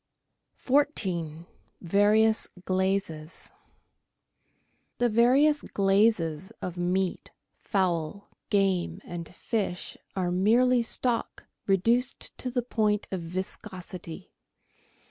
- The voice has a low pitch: No, high, 195 Hz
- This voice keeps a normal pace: No, slow, 85 wpm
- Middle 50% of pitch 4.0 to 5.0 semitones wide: Yes, average, 4.4 semitones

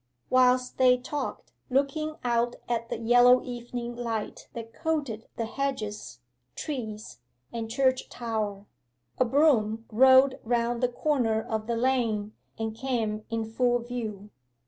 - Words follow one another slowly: Yes, slow, 130 wpm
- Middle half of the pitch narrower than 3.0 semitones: Yes, narrow, 2.5 semitones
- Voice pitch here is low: No, high, 240 Hz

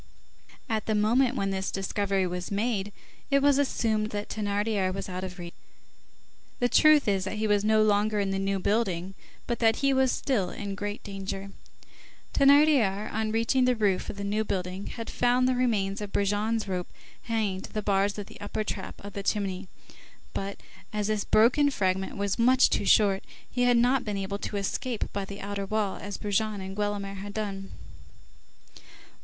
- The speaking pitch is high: Yes, high, 205 Hz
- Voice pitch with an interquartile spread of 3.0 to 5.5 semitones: No, narrow, 2.4 semitones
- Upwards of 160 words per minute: Yes, average, 185 wpm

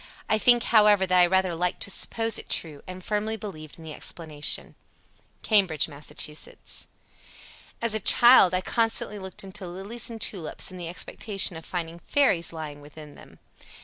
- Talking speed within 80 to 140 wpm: No, average, 170 wpm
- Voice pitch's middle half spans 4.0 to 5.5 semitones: Yes, average, 4.4 semitones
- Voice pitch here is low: No, medium, 185 Hz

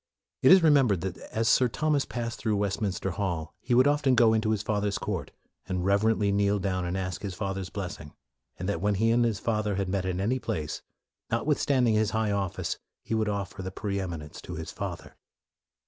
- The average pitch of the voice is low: Yes, low, 105 Hz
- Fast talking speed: Yes, fast, 210 wpm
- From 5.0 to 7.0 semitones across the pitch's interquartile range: No, average, 3.1 semitones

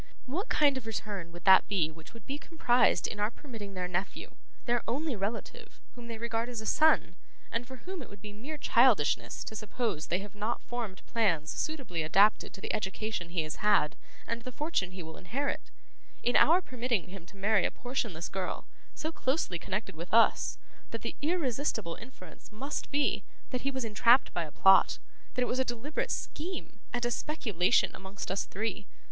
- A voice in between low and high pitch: No, high, 220 Hz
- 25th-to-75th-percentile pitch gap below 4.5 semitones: No, average, 5.1 semitones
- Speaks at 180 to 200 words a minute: Yes, average, 190 wpm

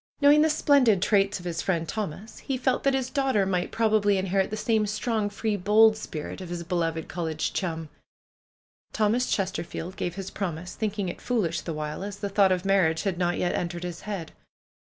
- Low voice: No, high, 195 Hz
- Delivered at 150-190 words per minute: No, average, 200 wpm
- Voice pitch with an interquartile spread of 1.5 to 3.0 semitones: No, average, 3.7 semitones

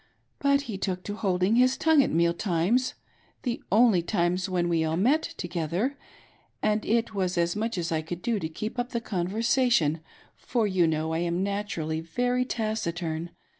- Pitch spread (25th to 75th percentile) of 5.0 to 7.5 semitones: Yes, wide, 5.4 semitones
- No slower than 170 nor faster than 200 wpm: Yes, average, 185 wpm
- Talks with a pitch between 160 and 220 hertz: Yes, high, 190 Hz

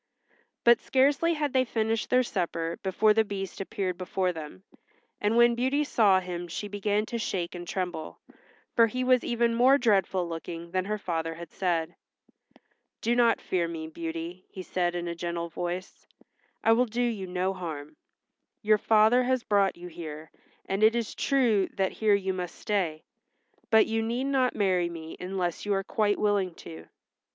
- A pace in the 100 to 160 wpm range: No, average, 175 wpm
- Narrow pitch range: No, average, 4.6 semitones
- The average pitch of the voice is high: Yes, high, 195 Hz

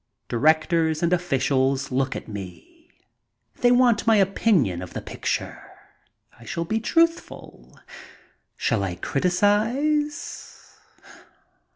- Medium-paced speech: No, slow, 100 wpm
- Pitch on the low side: No, medium, 170 Hz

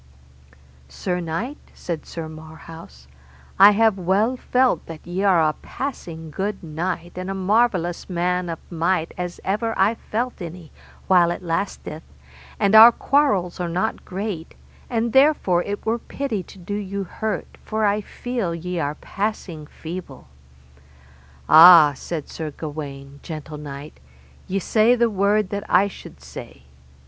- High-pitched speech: No, medium, 180 Hz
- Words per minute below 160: Yes, average, 145 wpm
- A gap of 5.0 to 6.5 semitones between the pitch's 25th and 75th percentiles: No, average, 4.4 semitones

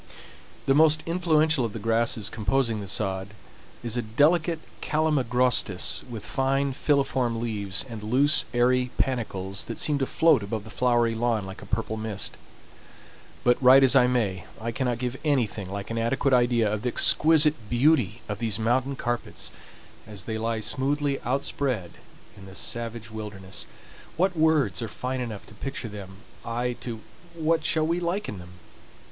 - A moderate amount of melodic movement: Yes, average, 4.1 semitones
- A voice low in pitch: Yes, low, 120 Hz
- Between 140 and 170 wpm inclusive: Yes, average, 160 wpm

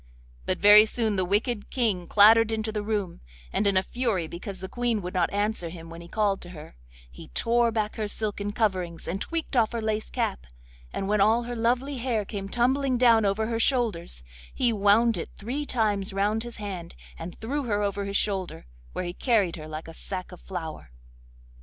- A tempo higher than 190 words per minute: Yes, average, 200 wpm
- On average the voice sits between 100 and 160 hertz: No, high, 210 Hz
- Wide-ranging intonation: No, average, 3.5 semitones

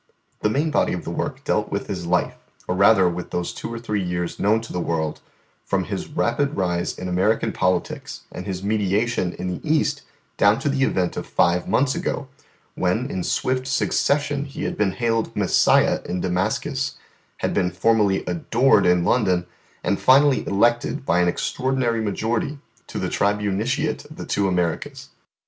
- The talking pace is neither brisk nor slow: Yes, average, 175 wpm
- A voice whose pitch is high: No, low, 105 Hz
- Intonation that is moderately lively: No, wide, 6.1 semitones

